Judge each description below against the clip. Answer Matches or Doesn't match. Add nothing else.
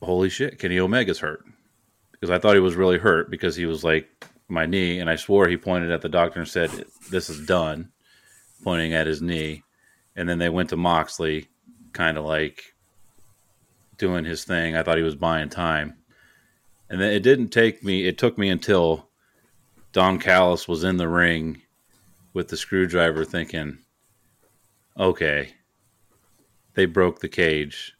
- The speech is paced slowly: Doesn't match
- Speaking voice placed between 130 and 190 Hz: Doesn't match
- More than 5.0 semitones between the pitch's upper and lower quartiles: Doesn't match